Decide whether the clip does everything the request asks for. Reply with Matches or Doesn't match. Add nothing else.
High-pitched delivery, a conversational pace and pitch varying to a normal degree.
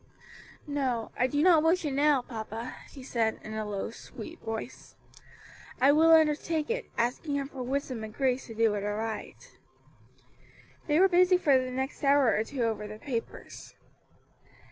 Matches